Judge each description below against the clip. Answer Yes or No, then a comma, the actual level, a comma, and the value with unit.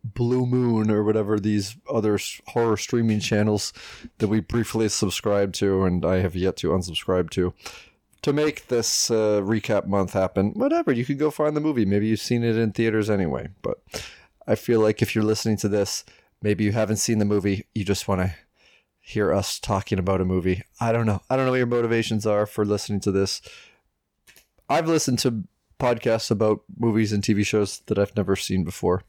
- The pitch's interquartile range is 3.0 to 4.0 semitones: No, narrow, 2.5 semitones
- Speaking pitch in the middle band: No, low, 105 Hz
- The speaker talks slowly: No, average, 195 wpm